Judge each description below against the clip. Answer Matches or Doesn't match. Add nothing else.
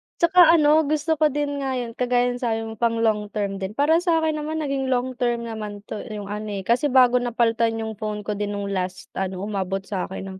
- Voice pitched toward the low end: Doesn't match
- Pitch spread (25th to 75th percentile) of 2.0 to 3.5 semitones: Doesn't match